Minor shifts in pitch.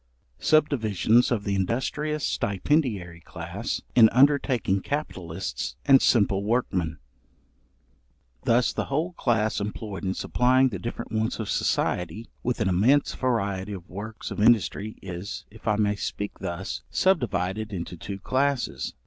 No: average, 4.6 semitones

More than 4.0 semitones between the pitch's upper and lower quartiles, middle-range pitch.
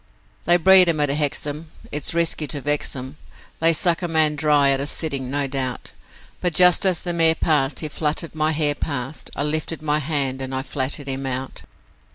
No: average, 2.8 semitones; medium, 150 Hz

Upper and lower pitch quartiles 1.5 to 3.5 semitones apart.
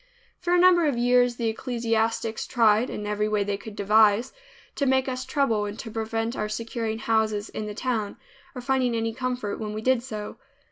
Yes: average, 2.8 semitones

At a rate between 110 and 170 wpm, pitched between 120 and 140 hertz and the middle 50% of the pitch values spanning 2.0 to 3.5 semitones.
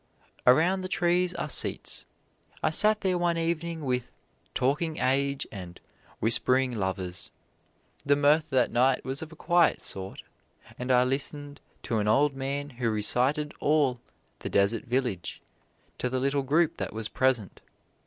No: average, 150 wpm; low, 135 Hz; average, 4.2 semitones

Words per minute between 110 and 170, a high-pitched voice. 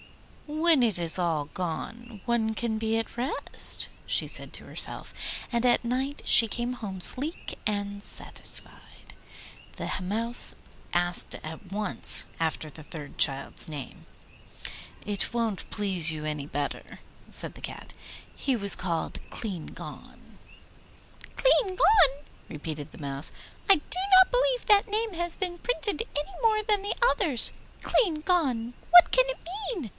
Yes: average, 140 wpm; high, 235 Hz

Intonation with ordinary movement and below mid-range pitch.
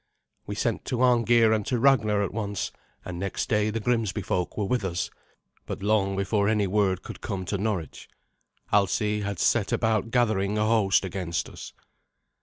No: narrow, 2.3 semitones; low, 105 Hz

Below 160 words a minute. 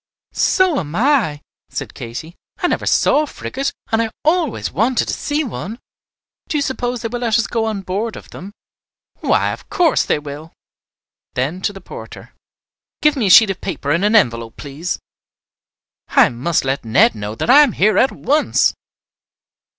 No: average, 180 wpm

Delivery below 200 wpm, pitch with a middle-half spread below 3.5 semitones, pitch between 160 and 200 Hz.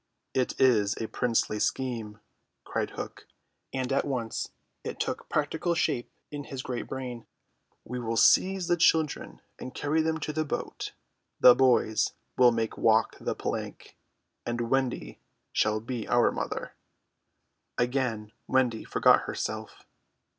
No: average, 140 wpm; average, 3.1 semitones; low, 125 Hz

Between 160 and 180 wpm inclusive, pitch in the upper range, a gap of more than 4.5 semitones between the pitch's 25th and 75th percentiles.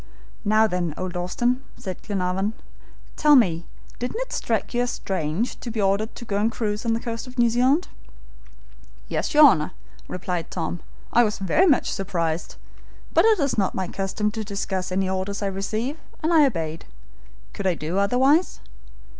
Yes: average, 175 wpm; high, 205 Hz; average, 4.9 semitones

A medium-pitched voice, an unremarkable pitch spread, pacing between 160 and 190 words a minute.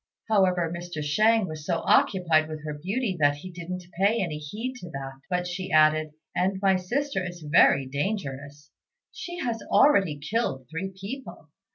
Yes: medium, 175 Hz; average, 4.5 semitones; average, 165 wpm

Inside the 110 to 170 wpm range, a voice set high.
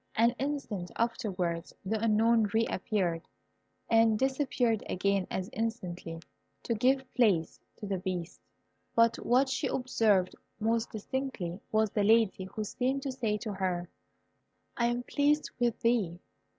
Yes: average, 140 wpm; high, 225 Hz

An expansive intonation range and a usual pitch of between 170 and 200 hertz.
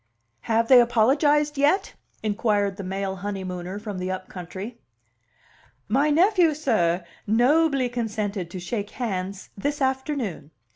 No: wide, 6.2 semitones; high, 220 Hz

